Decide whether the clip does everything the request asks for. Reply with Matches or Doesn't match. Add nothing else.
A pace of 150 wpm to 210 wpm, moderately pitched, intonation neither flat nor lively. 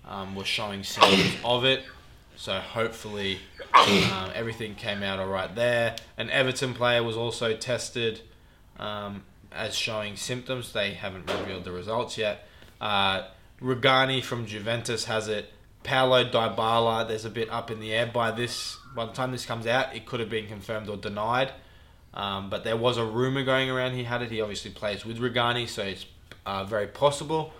Doesn't match